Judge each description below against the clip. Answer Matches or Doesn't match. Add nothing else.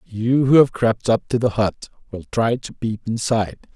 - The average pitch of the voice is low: Matches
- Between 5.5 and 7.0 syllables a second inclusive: Doesn't match